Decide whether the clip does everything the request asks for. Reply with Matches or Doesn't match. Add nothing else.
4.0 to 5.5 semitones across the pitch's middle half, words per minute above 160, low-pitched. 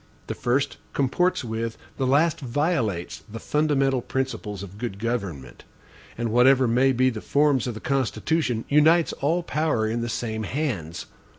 Doesn't match